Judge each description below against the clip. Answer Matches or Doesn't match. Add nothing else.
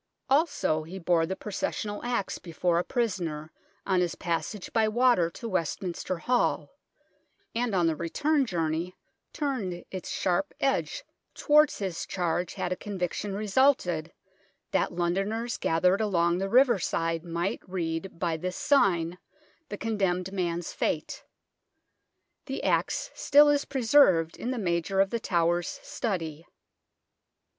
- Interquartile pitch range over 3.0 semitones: Matches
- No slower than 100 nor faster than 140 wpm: Matches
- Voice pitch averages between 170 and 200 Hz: Matches